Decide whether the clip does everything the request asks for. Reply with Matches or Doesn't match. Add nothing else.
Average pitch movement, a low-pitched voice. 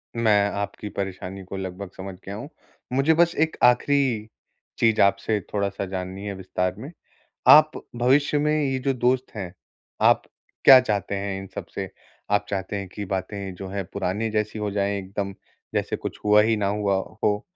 Matches